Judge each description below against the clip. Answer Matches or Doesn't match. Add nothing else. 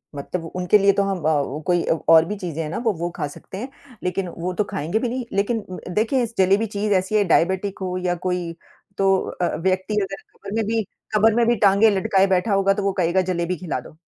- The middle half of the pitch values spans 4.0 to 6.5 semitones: Doesn't match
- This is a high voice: Matches